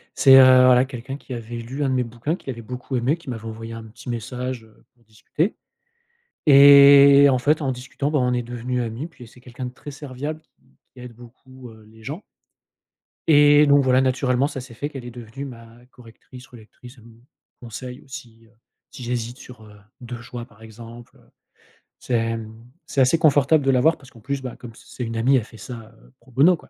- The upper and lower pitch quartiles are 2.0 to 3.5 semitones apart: Yes, average, 2.8 semitones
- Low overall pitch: Yes, low, 125 Hz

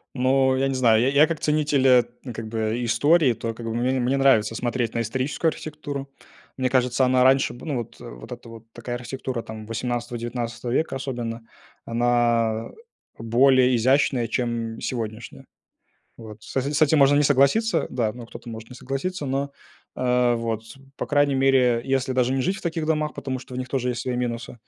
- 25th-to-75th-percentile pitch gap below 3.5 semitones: Yes, narrow, 2.5 semitones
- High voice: No, low, 125 Hz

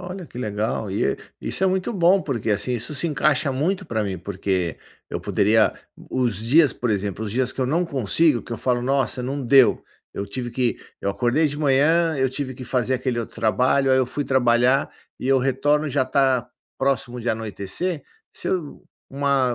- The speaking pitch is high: No, low, 130 Hz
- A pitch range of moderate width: Yes, average, 3.6 semitones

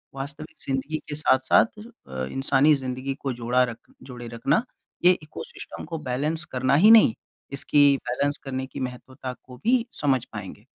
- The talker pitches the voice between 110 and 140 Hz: Yes, low, 135 Hz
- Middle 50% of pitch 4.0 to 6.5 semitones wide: No, average, 3.1 semitones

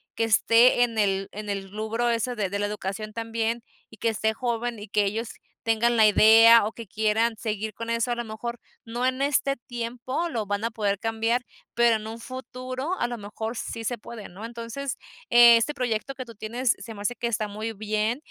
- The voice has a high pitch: Yes, high, 230 Hz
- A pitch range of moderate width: No, narrow, 1.9 semitones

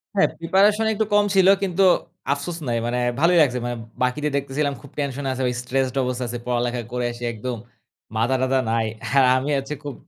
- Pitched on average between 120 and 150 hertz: Yes, low, 135 Hz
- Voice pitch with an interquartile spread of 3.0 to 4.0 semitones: Yes, average, 3.5 semitones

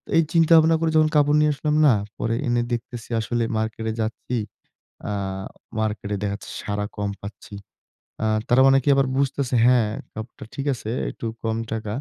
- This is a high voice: No, low, 120 Hz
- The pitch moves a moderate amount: Yes, average, 4.3 semitones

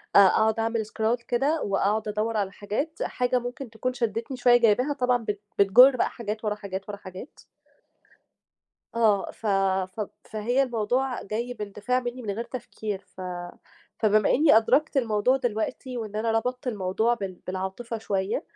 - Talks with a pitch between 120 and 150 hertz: No, high, 225 Hz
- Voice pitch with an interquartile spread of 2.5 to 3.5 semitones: Yes, average, 3.1 semitones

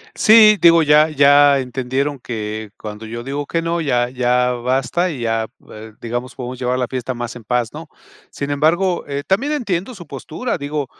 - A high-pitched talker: No, low, 135 Hz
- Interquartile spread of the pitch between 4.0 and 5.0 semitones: Yes, average, 4.7 semitones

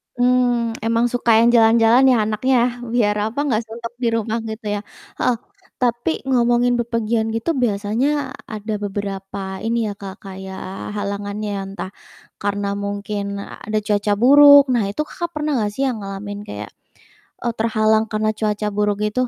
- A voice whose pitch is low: No, high, 220 Hz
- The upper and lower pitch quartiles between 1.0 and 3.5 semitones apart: Yes, average, 2.8 semitones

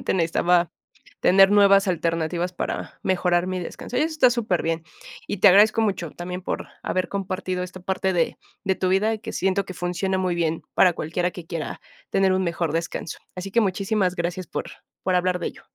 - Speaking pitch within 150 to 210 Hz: Yes, medium, 185 Hz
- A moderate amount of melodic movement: No, narrow, 1.8 semitones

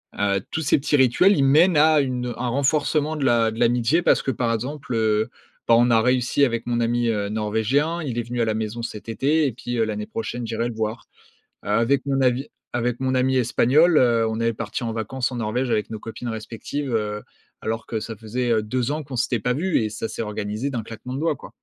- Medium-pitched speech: No, low, 120 Hz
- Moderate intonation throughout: Yes, average, 3.1 semitones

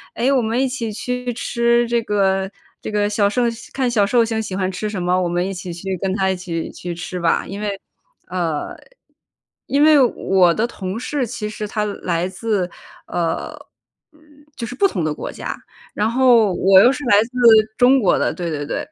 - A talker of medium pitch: No, high, 205 Hz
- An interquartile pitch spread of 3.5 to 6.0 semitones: Yes, average, 4.4 semitones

